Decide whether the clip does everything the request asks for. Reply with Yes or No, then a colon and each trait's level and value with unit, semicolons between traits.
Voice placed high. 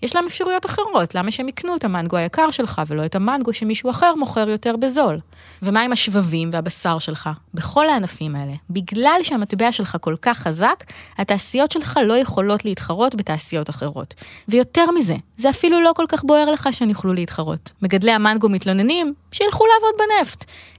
Yes: high, 220 Hz